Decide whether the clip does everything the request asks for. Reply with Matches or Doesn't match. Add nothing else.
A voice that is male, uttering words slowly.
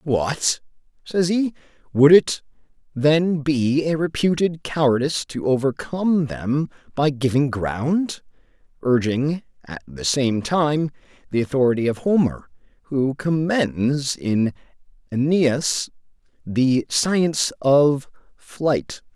Matches